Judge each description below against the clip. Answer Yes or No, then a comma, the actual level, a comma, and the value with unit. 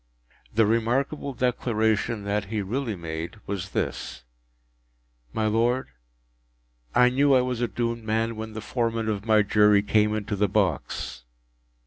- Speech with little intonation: Yes, narrow, 2.3 semitones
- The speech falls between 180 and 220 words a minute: No, average, 145 wpm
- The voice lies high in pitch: No, low, 110 Hz